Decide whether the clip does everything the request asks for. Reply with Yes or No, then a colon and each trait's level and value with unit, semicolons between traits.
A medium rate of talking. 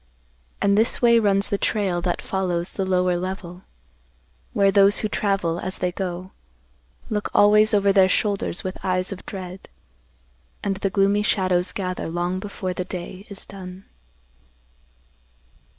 Yes: average, 145 wpm